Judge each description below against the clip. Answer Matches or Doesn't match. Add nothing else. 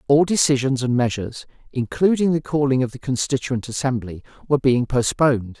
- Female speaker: Doesn't match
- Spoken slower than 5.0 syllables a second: Doesn't match